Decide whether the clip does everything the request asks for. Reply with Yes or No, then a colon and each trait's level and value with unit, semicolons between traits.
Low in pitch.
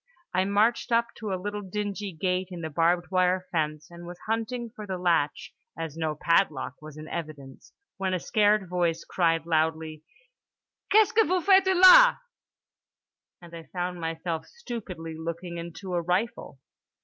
No: medium, 180 Hz